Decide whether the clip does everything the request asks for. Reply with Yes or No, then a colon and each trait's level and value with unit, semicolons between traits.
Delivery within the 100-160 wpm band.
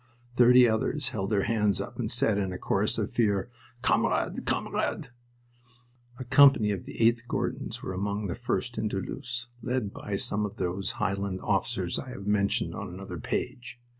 No: average, 170 wpm